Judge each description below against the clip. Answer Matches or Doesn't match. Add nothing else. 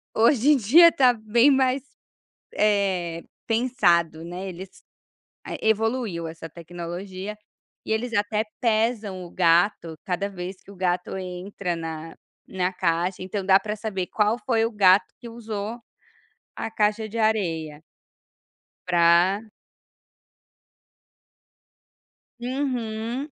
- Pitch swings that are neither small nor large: Matches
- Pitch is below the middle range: Doesn't match